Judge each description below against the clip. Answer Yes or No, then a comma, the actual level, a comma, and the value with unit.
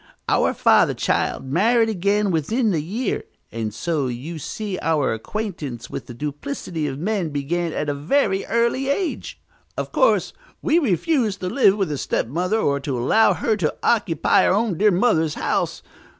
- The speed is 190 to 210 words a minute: No, average, 165 wpm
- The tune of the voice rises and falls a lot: Yes, wide, 7.0 semitones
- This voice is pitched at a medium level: Yes, medium, 180 Hz